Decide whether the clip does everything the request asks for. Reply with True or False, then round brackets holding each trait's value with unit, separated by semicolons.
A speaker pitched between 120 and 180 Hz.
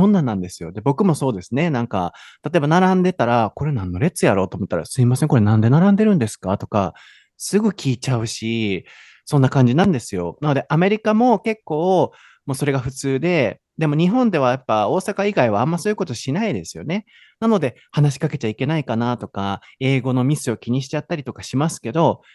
True (135 Hz)